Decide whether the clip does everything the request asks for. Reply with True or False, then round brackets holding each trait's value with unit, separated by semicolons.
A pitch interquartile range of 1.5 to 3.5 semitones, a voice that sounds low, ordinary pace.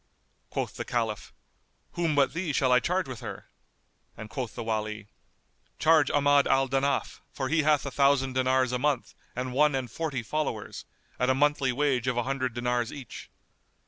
True (2.9 semitones; 130 Hz; 175 wpm)